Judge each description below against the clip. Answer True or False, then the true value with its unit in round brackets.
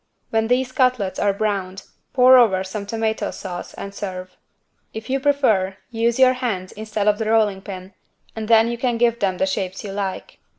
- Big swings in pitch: False (3.6 semitones)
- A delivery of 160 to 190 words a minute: True (185 wpm)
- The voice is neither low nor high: False (215 Hz)